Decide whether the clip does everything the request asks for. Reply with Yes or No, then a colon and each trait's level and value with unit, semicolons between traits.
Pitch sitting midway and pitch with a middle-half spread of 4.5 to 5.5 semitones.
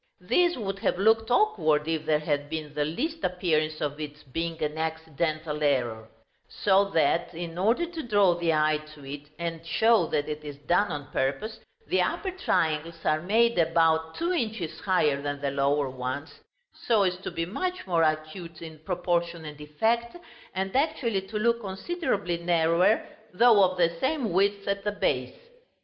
Yes: medium, 170 Hz; average, 5.1 semitones